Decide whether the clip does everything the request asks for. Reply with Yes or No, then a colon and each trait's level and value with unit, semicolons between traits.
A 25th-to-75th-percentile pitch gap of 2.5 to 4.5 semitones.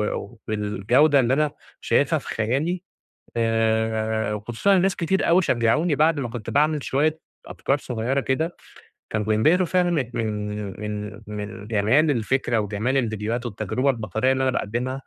No: average, 5.0 semitones